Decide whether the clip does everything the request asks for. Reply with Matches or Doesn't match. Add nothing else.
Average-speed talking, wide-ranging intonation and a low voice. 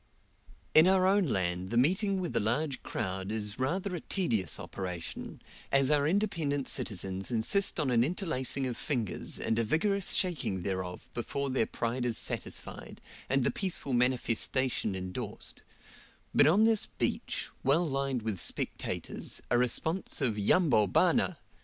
Matches